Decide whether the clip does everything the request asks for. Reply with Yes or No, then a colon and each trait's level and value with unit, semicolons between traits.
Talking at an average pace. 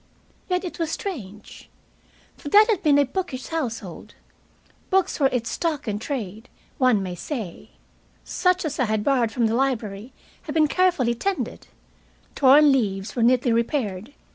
Yes: average, 155 wpm